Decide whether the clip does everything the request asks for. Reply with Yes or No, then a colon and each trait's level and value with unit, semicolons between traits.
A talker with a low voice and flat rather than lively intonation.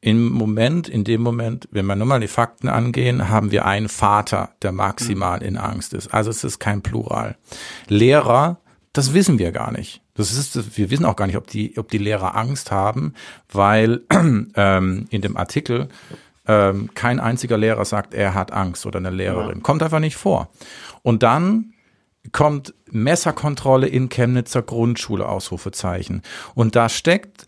No: low, 110 Hz; average, 3.7 semitones